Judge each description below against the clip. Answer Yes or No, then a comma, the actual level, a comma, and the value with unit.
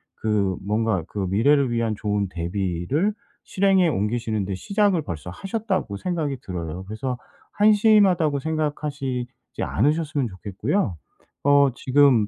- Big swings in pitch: Yes, wide, 7.8 semitones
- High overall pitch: No, low, 125 Hz